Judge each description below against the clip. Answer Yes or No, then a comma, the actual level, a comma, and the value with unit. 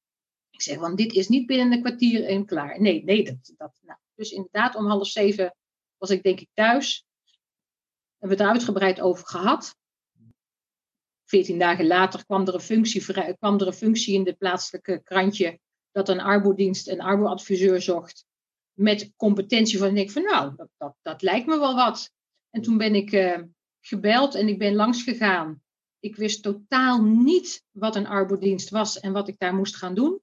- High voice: Yes, high, 200 Hz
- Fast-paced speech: No, average, 185 wpm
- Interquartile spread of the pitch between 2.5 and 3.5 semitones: Yes, average, 2.8 semitones